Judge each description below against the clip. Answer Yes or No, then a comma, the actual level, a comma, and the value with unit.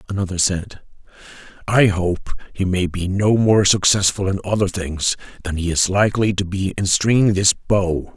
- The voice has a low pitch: Yes, very low, 95 Hz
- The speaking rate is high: No, average, 170 wpm